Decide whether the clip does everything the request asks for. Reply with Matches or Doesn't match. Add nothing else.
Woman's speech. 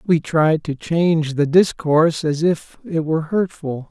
Doesn't match